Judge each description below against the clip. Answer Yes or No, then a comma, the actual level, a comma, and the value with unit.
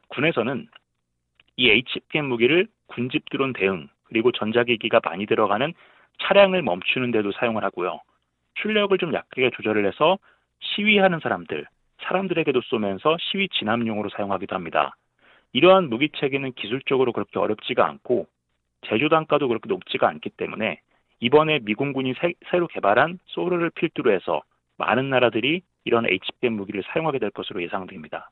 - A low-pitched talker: Yes, low, 130 Hz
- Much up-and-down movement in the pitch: Yes, wide, 8.1 semitones